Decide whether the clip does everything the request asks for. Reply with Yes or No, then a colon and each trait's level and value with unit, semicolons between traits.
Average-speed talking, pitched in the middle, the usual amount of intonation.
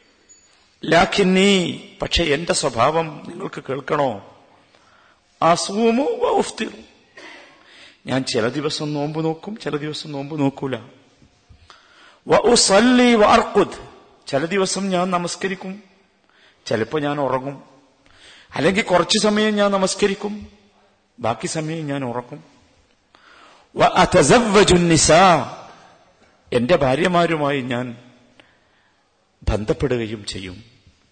No: average, 75 wpm; medium, 160 Hz; wide, 6.6 semitones